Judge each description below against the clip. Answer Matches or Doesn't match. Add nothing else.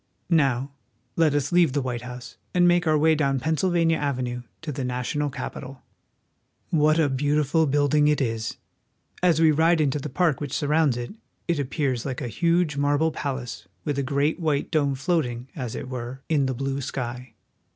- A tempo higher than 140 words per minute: Matches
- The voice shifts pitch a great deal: Doesn't match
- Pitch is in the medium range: Matches